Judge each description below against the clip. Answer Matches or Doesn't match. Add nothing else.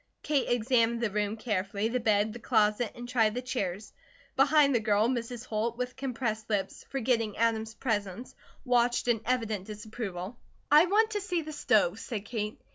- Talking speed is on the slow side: Doesn't match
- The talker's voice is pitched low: Doesn't match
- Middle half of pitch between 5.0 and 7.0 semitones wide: Doesn't match